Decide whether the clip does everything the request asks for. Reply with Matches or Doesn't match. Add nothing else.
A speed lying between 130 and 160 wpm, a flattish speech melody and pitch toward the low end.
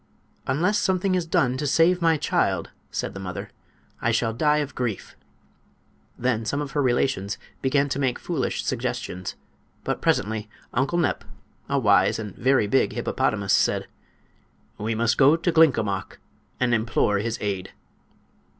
Doesn't match